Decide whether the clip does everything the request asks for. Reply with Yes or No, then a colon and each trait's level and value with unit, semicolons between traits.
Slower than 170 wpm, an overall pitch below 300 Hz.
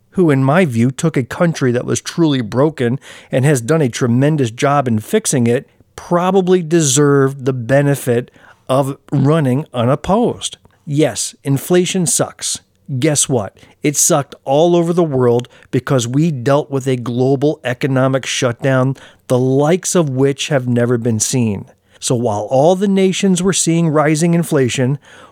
Yes: average, 150 wpm; medium, 140 Hz